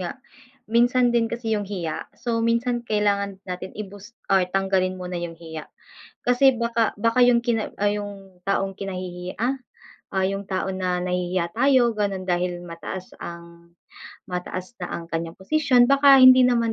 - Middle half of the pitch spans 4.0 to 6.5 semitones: Yes, average, 4.5 semitones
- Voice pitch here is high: Yes, high, 195 Hz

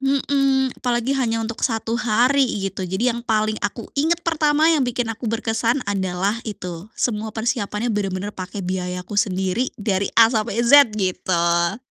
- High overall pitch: Yes, high, 225 Hz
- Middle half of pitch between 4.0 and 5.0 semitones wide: Yes, average, 4.3 semitones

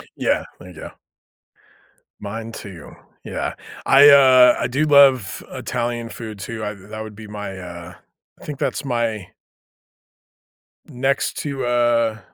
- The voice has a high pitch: No, low, 115 Hz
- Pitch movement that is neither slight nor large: Yes, average, 3.8 semitones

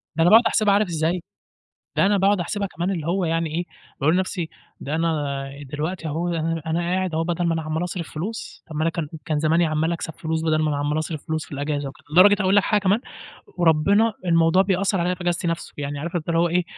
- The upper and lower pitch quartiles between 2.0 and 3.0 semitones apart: Yes, average, 2.7 semitones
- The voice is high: No, medium, 165 Hz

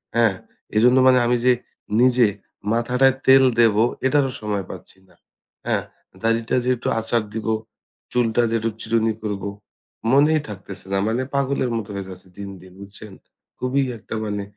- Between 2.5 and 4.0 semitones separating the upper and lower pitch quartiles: Yes, average, 3.6 semitones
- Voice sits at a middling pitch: No, low, 115 Hz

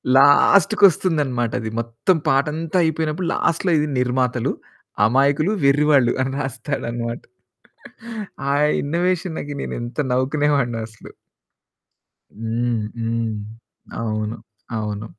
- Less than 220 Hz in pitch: Yes, low, 135 Hz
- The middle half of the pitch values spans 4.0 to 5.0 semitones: Yes, average, 4.6 semitones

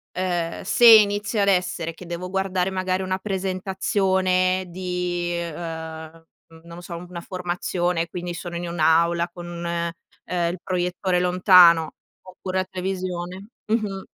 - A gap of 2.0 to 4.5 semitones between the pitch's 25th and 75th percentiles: No, narrow, 1.4 semitones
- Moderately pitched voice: Yes, medium, 180 Hz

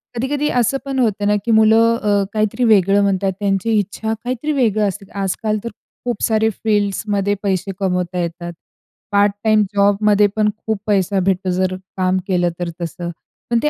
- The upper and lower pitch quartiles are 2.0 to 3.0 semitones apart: Yes, narrow, 2.4 semitones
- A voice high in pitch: Yes, high, 205 Hz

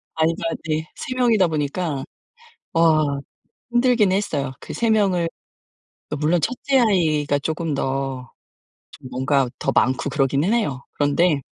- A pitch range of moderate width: Yes, average, 5.0 semitones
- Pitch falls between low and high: Yes, medium, 155 Hz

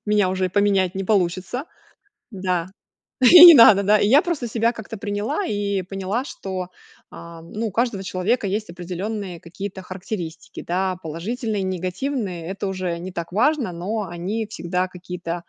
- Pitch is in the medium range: No, high, 195 Hz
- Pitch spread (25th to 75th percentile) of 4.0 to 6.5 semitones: No, average, 3.3 semitones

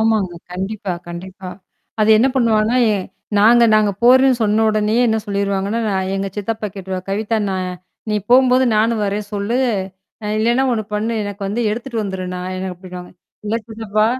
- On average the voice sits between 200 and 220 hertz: Yes, high, 210 Hz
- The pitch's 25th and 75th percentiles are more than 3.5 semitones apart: No, average, 2.8 semitones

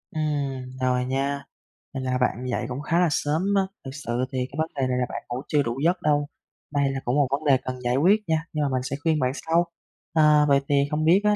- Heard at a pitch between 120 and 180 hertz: Yes, medium, 140 Hz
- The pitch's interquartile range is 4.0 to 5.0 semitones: No, average, 3.2 semitones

